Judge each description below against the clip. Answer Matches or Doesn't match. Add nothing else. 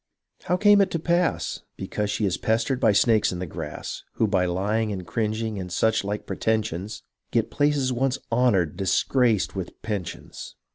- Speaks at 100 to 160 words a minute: Doesn't match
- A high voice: Doesn't match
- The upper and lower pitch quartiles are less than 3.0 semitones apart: Doesn't match